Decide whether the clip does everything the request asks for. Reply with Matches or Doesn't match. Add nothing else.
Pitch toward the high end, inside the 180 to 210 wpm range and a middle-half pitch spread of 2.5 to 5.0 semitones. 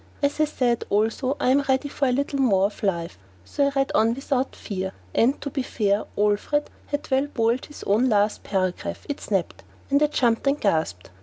Doesn't match